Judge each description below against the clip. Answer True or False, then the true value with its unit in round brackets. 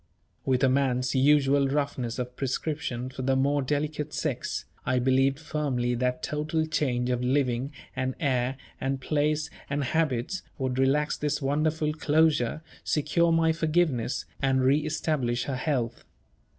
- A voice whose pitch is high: False (140 Hz)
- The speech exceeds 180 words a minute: False (140 wpm)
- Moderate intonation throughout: True (3.0 semitones)